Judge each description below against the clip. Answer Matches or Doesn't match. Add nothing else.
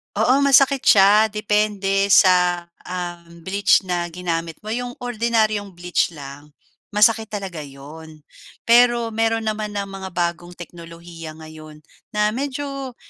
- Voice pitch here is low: Doesn't match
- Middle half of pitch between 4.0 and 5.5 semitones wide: Matches